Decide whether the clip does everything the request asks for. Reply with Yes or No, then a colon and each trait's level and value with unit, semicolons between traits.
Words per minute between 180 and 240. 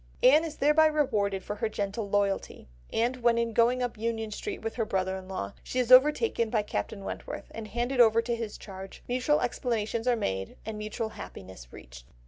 Yes: average, 195 wpm